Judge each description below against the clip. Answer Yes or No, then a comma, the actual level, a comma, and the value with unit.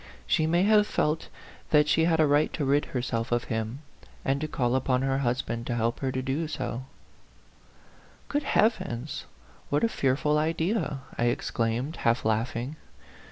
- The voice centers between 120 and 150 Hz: Yes, low, 135 Hz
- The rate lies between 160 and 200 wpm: Yes, average, 170 wpm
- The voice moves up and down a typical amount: Yes, average, 4.5 semitones